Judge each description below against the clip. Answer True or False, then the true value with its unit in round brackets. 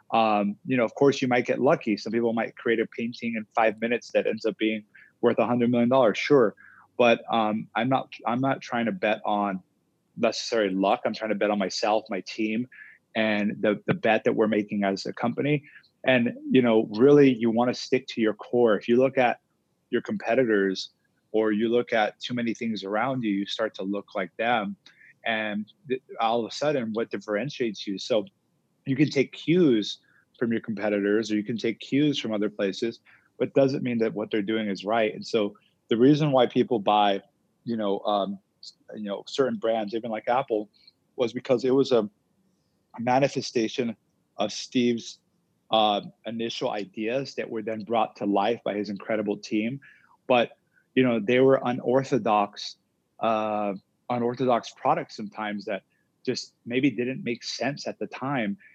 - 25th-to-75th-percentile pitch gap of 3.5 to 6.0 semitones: False (2.9 semitones)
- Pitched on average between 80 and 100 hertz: False (115 Hz)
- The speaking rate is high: False (185 wpm)